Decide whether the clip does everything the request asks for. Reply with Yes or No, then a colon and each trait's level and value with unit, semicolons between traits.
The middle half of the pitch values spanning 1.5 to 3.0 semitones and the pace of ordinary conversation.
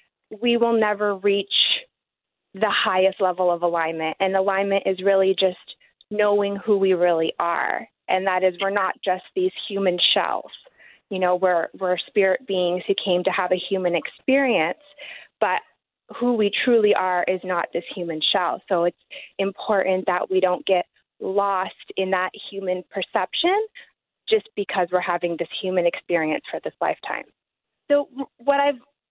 Yes: narrow, 2.5 semitones; average, 155 wpm